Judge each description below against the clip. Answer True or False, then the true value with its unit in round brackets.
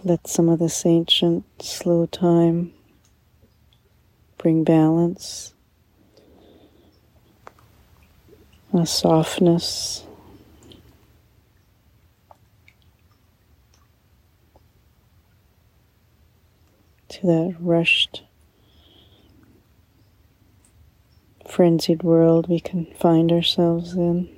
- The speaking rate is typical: False (50 wpm)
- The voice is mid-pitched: True (160 Hz)